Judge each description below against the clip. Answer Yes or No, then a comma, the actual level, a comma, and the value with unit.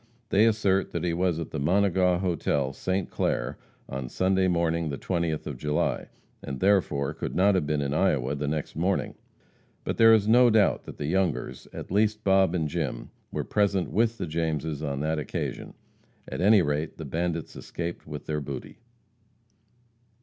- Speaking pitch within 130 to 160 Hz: No, very low, 85 Hz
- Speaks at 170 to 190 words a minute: Yes, average, 175 wpm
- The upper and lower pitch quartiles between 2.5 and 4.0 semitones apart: No, average, 4.4 semitones